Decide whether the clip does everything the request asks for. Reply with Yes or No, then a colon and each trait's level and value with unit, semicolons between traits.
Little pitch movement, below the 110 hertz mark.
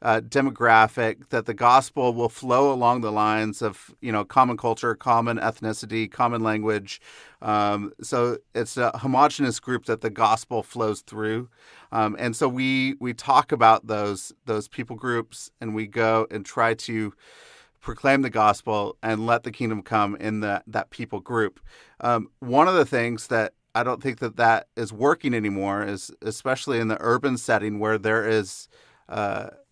No: narrow, 2.1 semitones; low, 115 Hz